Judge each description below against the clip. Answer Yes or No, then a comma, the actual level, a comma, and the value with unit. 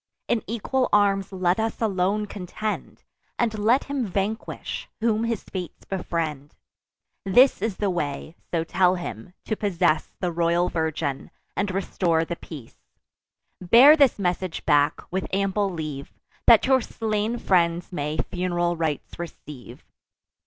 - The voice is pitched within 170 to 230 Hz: Yes, medium, 185 Hz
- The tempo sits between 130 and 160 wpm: Yes, slow, 135 wpm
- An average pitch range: Yes, average, 4.1 semitones